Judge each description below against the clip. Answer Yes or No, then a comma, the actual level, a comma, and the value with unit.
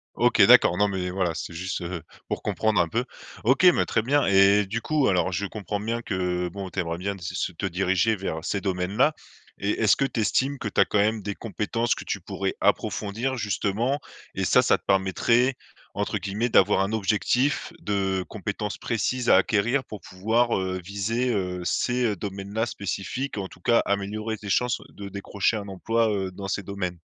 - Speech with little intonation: No, average, 3.1 semitones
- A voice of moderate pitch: No, low, 100 Hz